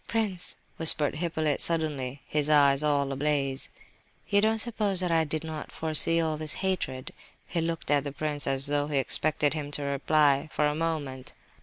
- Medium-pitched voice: Yes, medium, 150 Hz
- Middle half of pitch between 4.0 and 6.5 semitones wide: No, narrow, 2.5 semitones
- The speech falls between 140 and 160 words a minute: No, average, 175 wpm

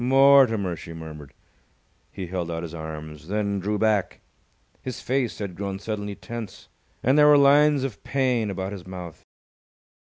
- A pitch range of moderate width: No, wide, 6.5 semitones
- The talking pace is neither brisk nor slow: Yes, average, 155 wpm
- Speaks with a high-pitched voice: No, low, 100 Hz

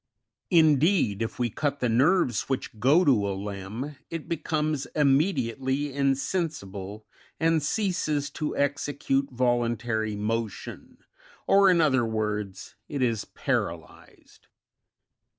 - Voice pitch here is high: No, low, 135 Hz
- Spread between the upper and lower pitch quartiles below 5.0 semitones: No, average, 5.3 semitones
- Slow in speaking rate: Yes, slow, 115 wpm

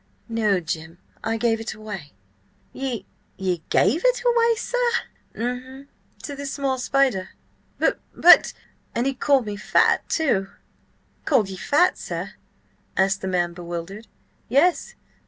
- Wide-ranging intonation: Yes, wide, 6.5 semitones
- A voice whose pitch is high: Yes, high, 230 Hz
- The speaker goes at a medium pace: No, slow, 130 wpm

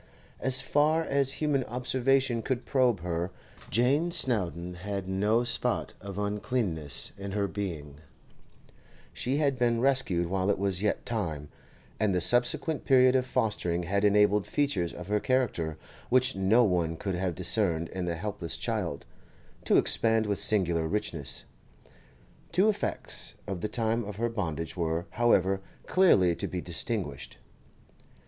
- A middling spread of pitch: No, wide, 5.9 semitones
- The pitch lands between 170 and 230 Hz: No, low, 105 Hz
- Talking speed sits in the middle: Yes, average, 145 wpm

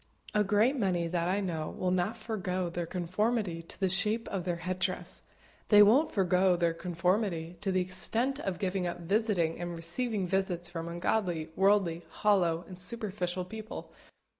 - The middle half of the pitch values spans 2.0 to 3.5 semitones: Yes, average, 3.2 semitones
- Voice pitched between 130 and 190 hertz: Yes, medium, 185 Hz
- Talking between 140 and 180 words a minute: Yes, average, 165 wpm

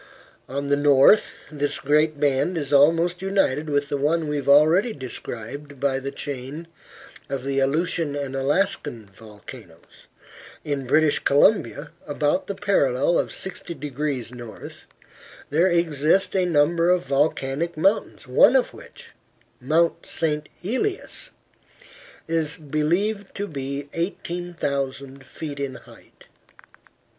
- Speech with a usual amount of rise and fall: Yes, average, 3.6 semitones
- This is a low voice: No, medium, 150 Hz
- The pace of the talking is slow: Yes, slow, 125 wpm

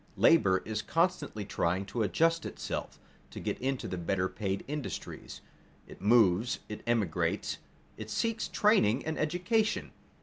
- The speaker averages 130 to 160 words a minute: Yes, slow, 135 wpm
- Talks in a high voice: No, low, 115 Hz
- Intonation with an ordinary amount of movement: No, wide, 8.8 semitones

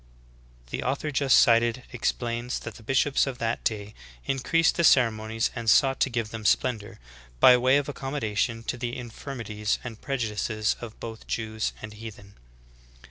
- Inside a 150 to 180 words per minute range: Yes, average, 160 wpm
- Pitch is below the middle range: Yes, low, 115 Hz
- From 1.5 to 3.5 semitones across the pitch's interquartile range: Yes, average, 3.0 semitones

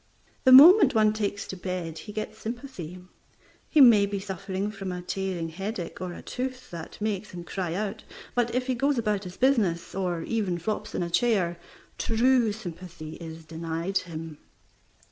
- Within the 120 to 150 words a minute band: No, average, 170 wpm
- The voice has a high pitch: Yes, high, 195 Hz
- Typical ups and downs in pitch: Yes, average, 4.4 semitones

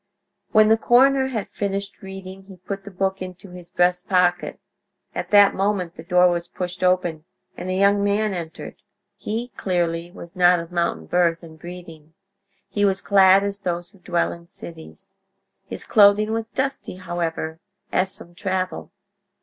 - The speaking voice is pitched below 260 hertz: Yes, medium, 185 Hz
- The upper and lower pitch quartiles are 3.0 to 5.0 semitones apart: No, narrow, 2.6 semitones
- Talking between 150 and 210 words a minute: Yes, average, 165 wpm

